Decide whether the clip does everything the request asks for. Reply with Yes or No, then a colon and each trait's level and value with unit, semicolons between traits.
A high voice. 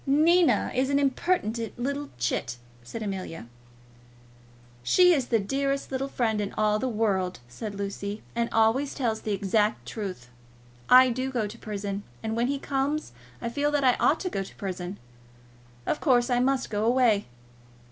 Yes: high, 230 Hz